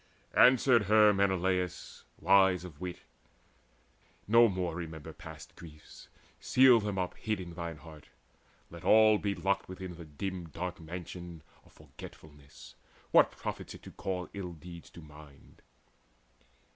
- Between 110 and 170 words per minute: Yes, slow, 135 wpm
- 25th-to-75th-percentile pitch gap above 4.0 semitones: No, average, 3.3 semitones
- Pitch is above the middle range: No, very low, 90 Hz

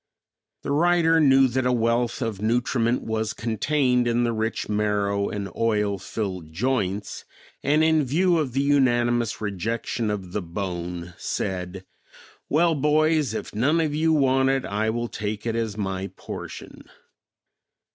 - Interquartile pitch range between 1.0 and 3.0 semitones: No, average, 4.8 semitones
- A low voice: Yes, low, 115 Hz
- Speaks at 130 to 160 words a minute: Yes, average, 145 wpm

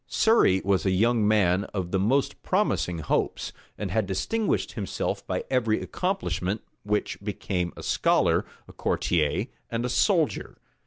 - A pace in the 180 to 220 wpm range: No, average, 145 wpm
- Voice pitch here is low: Yes, low, 100 Hz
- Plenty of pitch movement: No, average, 3.7 semitones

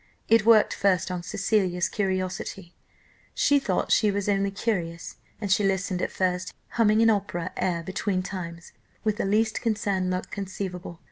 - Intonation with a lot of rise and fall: No, narrow, 2.4 semitones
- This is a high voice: Yes, high, 195 Hz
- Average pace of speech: Yes, average, 155 wpm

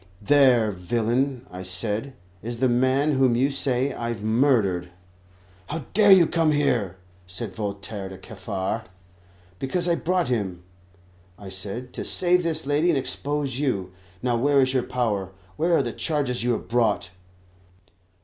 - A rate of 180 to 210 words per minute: No, average, 155 wpm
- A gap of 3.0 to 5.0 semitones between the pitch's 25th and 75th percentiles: No, wide, 5.5 semitones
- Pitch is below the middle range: Yes, low, 125 Hz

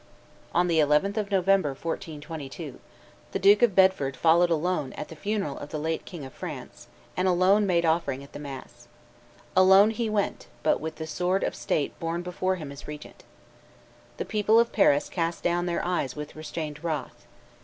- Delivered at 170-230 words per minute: Yes, average, 180 wpm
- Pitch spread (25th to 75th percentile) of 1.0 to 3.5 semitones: No, average, 4.1 semitones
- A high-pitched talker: No, medium, 170 Hz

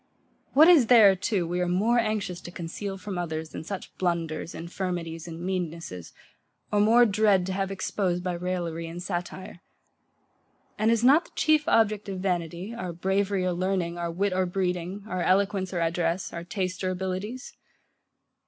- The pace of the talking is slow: No, average, 170 wpm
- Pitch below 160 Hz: No, medium, 185 Hz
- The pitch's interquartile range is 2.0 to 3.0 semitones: Yes, narrow, 2.6 semitones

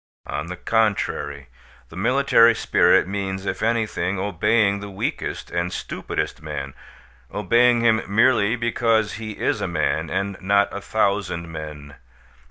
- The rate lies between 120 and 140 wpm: Yes, slow, 135 wpm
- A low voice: Yes, low, 100 Hz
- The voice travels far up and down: No, average, 4.4 semitones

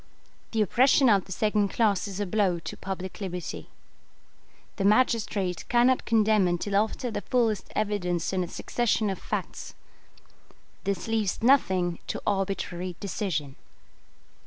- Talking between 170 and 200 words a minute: No, slow, 135 wpm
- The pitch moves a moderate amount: Yes, average, 3.0 semitones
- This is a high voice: Yes, high, 200 Hz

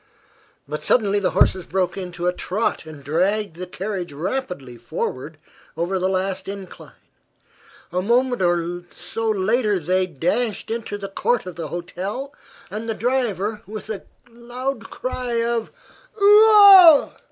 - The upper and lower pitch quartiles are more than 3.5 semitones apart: Yes, average, 4.8 semitones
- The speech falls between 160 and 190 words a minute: No, slow, 135 wpm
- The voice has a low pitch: No, high, 200 Hz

